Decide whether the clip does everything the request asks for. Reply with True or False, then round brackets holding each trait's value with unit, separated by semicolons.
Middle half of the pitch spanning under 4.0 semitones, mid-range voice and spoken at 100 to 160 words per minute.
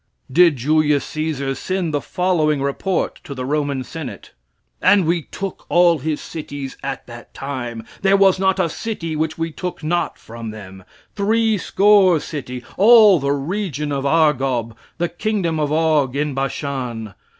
False (4.7 semitones; 155 Hz; 155 wpm)